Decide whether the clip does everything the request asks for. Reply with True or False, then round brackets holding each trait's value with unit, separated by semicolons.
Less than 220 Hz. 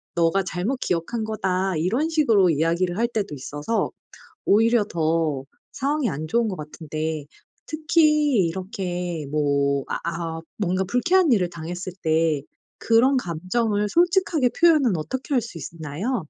True (190 Hz)